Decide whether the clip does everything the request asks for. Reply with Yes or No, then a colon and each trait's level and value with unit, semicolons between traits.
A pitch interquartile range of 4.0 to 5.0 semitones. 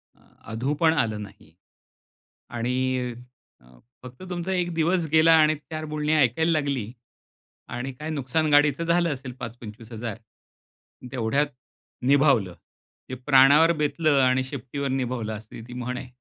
Yes: average, 4.3 semitones